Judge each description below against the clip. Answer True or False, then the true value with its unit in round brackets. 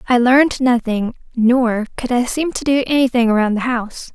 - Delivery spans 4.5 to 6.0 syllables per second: True (5.3 syllables/s)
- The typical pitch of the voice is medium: False (245 Hz)